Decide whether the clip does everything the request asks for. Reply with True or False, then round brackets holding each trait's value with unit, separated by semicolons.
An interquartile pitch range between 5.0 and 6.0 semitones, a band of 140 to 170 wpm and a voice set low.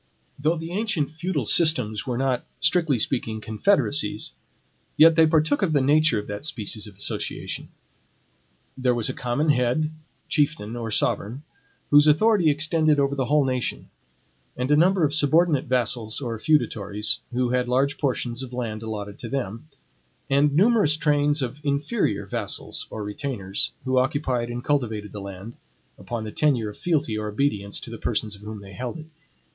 True (5.4 semitones; 165 wpm; 130 Hz)